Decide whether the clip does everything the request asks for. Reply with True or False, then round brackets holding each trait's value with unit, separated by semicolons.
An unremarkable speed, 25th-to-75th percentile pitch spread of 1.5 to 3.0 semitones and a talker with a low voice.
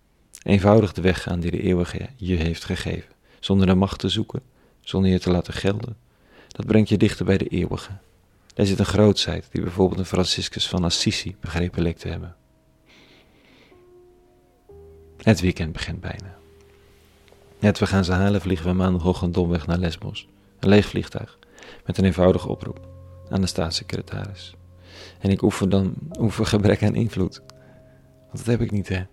True (170 wpm; 2.6 semitones; 95 Hz)